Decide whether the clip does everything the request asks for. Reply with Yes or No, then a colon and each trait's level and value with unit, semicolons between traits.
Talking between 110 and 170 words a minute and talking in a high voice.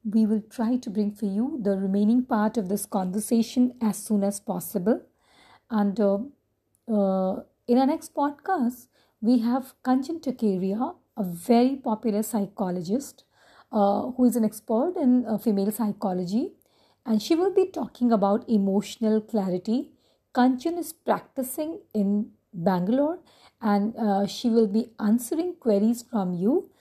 Yes: average, 140 wpm; high, 225 Hz